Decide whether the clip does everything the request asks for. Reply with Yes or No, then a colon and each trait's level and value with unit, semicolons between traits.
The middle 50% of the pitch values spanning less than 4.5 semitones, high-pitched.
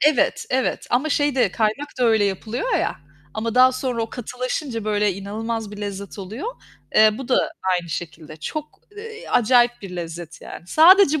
No: average, 4.8 semitones; high, 230 Hz